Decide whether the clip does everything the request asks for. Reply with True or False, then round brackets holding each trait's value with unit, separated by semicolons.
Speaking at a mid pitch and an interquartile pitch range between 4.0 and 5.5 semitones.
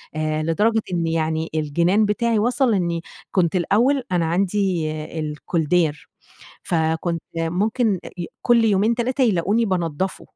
True (180 Hz; 5.0 semitones)